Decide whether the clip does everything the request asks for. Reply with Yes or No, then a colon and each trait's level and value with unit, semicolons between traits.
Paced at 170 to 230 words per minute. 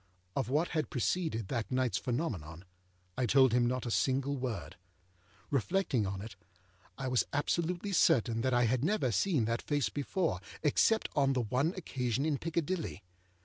No: average, 160 wpm